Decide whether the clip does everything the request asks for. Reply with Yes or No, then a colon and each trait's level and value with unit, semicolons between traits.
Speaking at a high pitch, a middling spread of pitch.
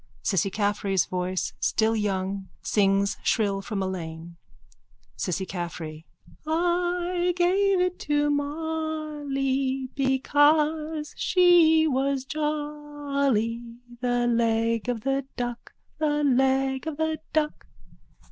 No: very high, 270 Hz; wide, 6.2 semitones